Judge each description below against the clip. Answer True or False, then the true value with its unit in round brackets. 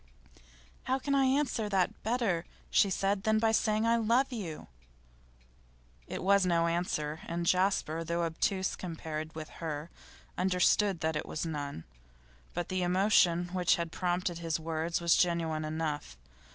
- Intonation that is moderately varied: True (3.6 semitones)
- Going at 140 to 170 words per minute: True (150 wpm)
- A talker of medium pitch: True (175 Hz)